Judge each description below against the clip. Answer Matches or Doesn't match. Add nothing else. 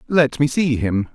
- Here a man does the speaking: Matches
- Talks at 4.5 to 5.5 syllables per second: Doesn't match